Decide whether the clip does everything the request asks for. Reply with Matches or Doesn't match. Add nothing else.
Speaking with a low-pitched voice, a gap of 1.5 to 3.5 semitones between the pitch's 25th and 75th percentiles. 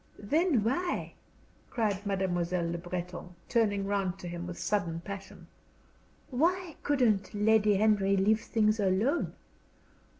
Doesn't match